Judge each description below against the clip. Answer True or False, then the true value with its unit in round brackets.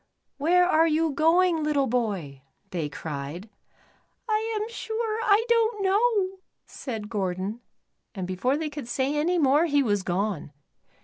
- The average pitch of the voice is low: False (295 Hz)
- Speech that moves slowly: False (145 wpm)